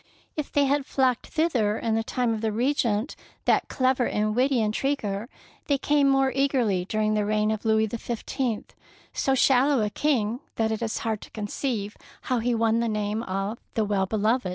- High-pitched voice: Yes, high, 225 Hz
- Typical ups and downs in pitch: Yes, average, 3.8 semitones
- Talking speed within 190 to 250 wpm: Yes, average, 195 wpm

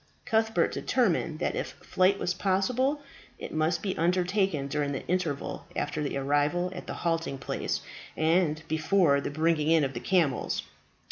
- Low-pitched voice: No, medium, 165 Hz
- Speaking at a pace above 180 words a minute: No, average, 155 wpm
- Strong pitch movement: No, average, 4.1 semitones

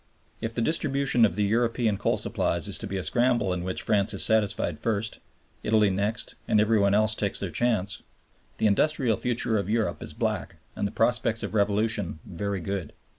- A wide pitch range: No, narrow, 2.4 semitones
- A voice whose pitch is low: Yes, low, 110 Hz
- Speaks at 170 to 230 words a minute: Yes, average, 190 wpm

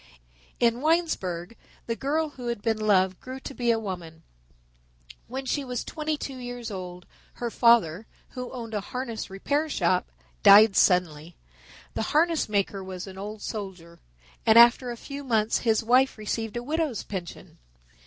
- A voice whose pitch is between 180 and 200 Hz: No, high, 225 Hz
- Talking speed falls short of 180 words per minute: Yes, average, 160 wpm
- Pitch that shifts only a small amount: No, average, 5.0 semitones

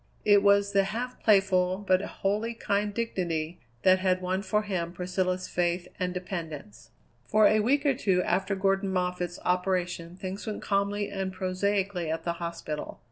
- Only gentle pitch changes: Yes, narrow, 2.0 semitones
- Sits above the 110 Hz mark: Yes, medium, 185 Hz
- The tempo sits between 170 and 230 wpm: No, average, 160 wpm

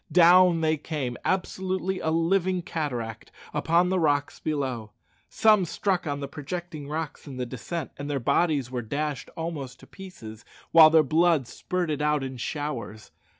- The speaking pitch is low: No, medium, 155 Hz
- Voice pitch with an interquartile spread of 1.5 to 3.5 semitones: No, average, 4.2 semitones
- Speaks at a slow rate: No, average, 155 wpm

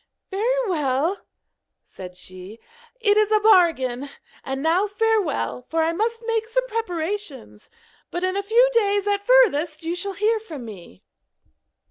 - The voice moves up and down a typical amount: No, wide, 6.8 semitones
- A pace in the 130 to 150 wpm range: Yes, average, 145 wpm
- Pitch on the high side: Yes, very high, 385 Hz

